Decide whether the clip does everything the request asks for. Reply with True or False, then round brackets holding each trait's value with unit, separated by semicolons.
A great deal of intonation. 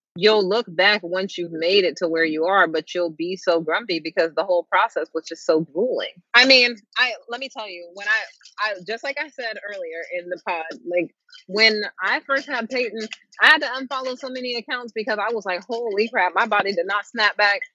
True (6.0 semitones)